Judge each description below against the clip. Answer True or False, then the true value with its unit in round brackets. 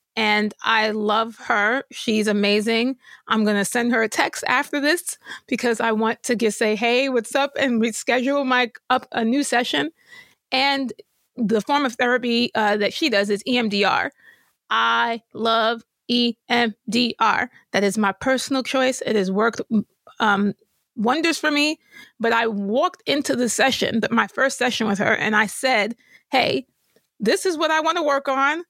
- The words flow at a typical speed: True (165 wpm)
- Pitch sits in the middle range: False (235 Hz)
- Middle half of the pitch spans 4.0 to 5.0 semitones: False (3.5 semitones)